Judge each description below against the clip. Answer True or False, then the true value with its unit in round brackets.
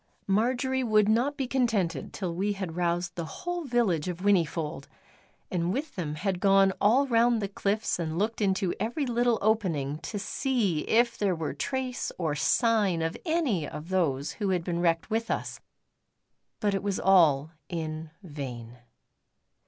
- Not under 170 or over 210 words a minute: False (160 wpm)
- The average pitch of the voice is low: False (195 Hz)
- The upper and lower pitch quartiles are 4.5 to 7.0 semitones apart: True (5.6 semitones)